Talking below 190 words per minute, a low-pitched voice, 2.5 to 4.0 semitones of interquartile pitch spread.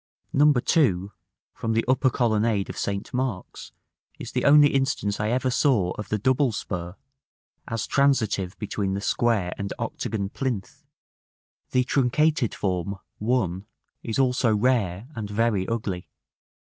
No: slow, 135 wpm; low, 110 Hz; average, 4.6 semitones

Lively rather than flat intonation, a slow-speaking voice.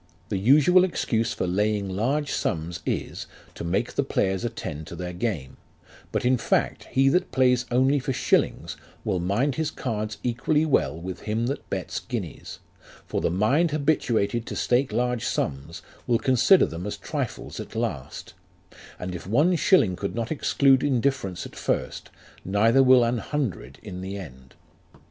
No: wide, 6.3 semitones; average, 165 wpm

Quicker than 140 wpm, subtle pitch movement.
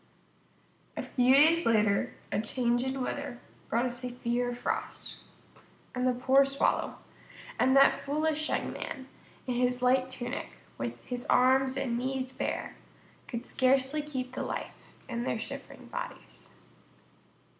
No: slow, 135 wpm; narrow, 1.7 semitones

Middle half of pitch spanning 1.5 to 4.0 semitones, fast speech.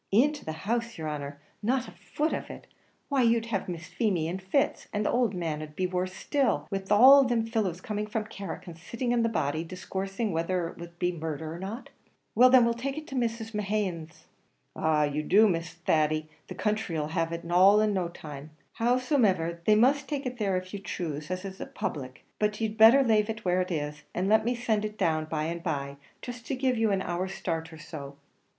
No: wide, 5.6 semitones; fast, 220 wpm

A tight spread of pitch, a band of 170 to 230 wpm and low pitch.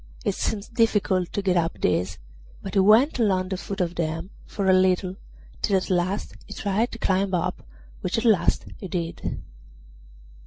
No: narrow, 2.3 semitones; average, 180 wpm; high, 190 Hz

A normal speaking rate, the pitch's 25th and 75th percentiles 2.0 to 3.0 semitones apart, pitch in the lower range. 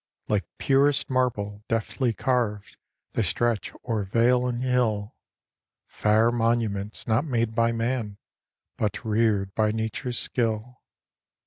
No: slow, 115 wpm; average, 2.7 semitones; low, 115 Hz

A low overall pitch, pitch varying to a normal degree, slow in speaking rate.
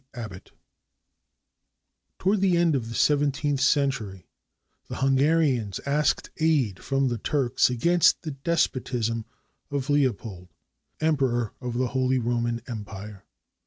Yes: low, 130 Hz; average, 4.0 semitones; slow, 125 wpm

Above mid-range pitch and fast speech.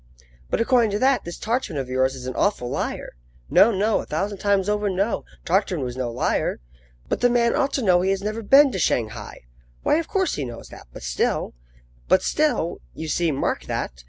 Yes: high, 195 Hz; fast, 215 wpm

